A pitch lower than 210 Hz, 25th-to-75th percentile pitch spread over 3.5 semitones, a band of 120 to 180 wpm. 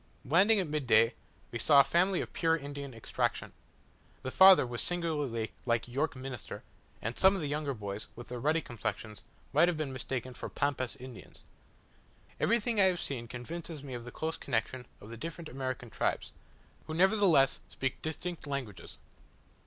Yes: medium, 140 Hz; average, 5.1 semitones; average, 170 wpm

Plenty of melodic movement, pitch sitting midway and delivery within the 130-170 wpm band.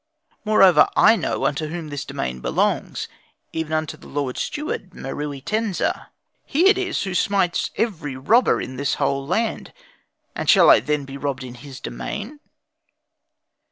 Yes: wide, 7.4 semitones; medium, 155 Hz; average, 150 wpm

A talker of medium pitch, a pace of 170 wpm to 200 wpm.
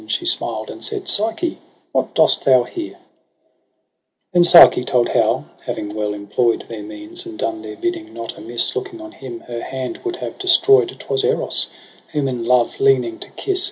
No: very high, 325 Hz; average, 175 wpm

